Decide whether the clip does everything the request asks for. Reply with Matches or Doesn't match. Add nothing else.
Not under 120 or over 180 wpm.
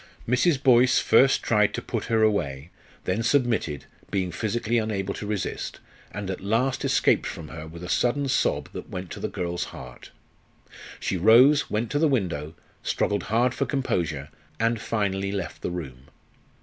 Matches